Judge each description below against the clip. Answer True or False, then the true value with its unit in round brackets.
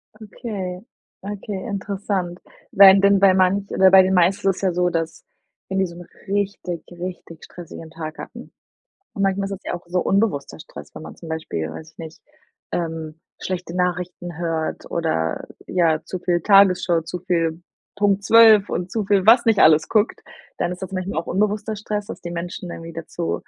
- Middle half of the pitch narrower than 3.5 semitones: True (2.9 semitones)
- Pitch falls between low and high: True (180 Hz)